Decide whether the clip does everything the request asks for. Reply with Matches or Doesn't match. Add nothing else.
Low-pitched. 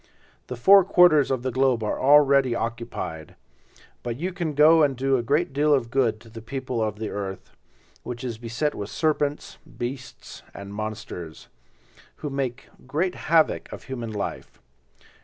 Matches